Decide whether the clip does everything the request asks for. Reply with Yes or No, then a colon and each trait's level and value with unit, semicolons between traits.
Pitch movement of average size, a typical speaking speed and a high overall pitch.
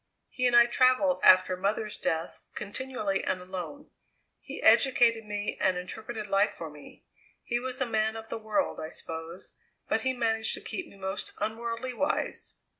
Yes: average, 4.5 semitones; average, 170 wpm; high, 220 Hz